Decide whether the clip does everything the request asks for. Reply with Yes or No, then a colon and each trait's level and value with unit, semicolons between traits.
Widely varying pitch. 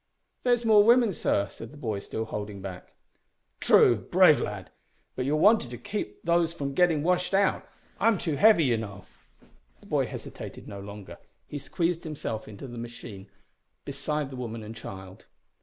Yes: wide, 8.2 semitones